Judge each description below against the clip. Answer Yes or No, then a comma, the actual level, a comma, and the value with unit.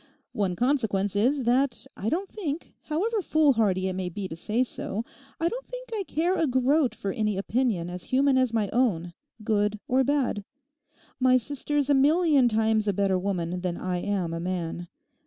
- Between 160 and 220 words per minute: Yes, average, 180 wpm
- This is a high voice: Yes, high, 230 Hz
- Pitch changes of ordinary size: No, wide, 6.7 semitones